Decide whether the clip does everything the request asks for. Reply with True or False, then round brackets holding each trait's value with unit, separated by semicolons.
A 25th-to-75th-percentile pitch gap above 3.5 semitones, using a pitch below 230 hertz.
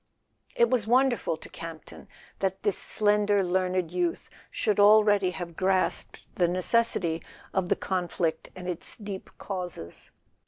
False (2.8 semitones; 190 Hz)